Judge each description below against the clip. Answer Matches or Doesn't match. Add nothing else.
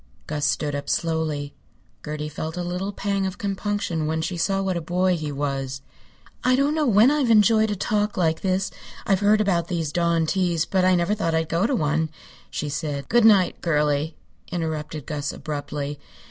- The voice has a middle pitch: Matches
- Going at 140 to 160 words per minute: Doesn't match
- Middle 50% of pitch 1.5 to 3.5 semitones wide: Doesn't match